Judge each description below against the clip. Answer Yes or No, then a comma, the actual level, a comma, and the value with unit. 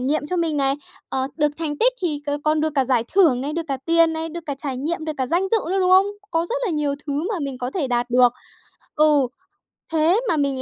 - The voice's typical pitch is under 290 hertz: No, very high, 300 Hz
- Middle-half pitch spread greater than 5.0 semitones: No, average, 3.6 semitones